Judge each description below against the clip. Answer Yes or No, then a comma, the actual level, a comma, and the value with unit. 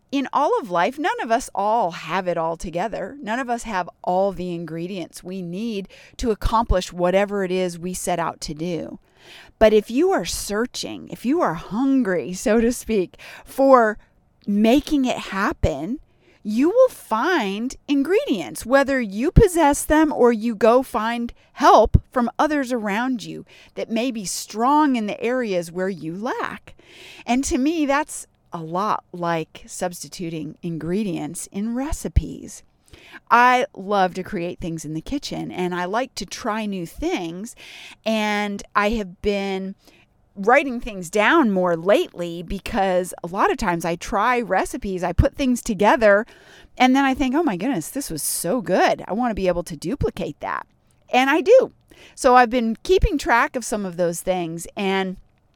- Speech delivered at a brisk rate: No, average, 165 wpm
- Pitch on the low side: No, high, 210 Hz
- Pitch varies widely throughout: Yes, wide, 5.7 semitones